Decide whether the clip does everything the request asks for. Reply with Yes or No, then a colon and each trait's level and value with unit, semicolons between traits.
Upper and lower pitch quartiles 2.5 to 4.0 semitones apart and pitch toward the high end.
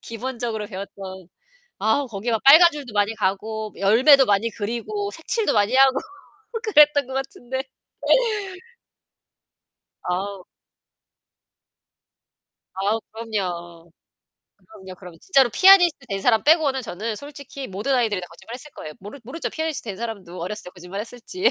No: wide, 5.5 semitones; high, 225 Hz